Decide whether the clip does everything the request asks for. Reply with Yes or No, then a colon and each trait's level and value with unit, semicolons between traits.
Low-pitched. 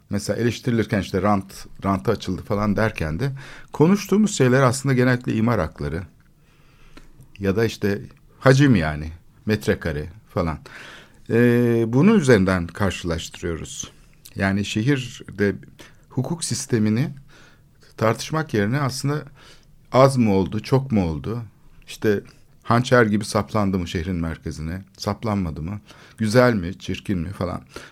Yes: low, 110 Hz